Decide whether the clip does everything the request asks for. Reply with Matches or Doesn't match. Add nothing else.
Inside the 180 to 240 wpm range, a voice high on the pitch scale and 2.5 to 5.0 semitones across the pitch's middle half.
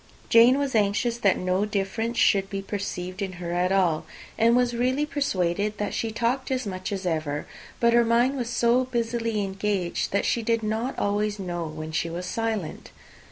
Matches